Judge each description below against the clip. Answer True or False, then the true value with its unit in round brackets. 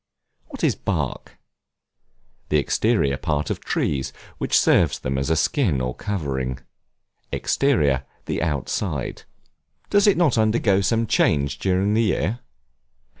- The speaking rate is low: True (125 wpm)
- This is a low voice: True (80 Hz)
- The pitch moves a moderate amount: False (8.1 semitones)